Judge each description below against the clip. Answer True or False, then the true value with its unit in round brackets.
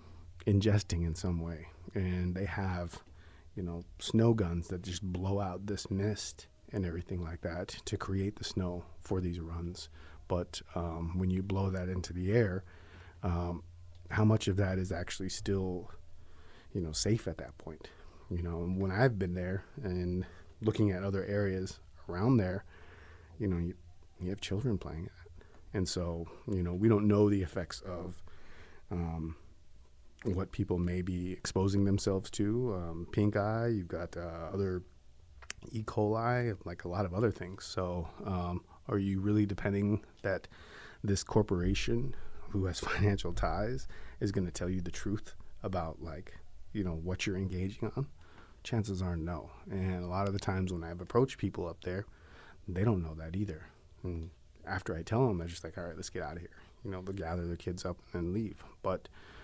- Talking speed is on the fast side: False (180 wpm)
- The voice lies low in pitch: True (90 Hz)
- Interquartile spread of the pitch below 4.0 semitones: True (2.8 semitones)